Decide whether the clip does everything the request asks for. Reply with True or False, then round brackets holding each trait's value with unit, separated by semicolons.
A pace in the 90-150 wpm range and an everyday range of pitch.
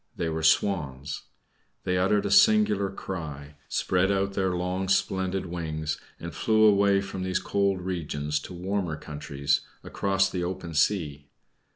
True (145 wpm; 3.9 semitones)